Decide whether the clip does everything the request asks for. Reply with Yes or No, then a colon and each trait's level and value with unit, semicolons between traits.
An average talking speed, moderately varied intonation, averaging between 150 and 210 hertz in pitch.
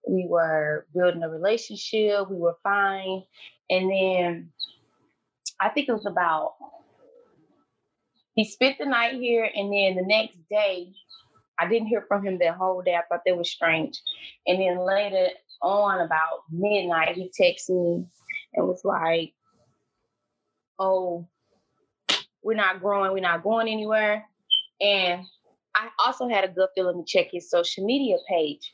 Yes: average, 150 wpm; average, 3.7 semitones; high, 190 Hz